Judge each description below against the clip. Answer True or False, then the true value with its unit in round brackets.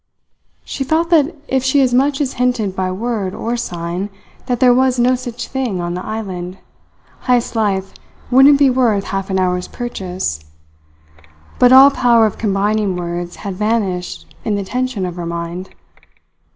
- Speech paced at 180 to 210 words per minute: False (165 wpm)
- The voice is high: True (215 Hz)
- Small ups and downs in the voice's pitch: False (5.3 semitones)